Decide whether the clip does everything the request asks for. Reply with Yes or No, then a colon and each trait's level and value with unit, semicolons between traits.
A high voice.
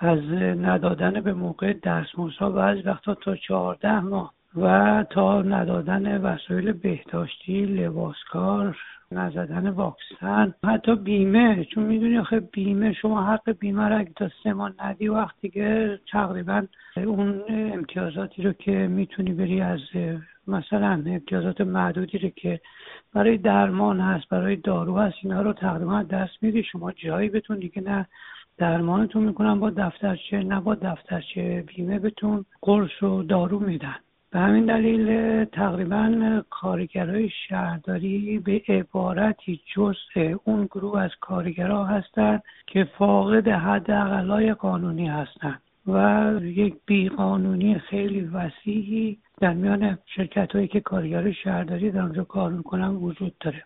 Yes: high, 195 Hz